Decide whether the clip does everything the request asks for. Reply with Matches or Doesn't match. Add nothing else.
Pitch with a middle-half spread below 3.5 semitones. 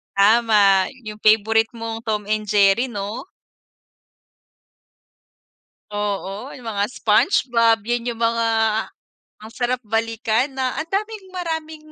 Matches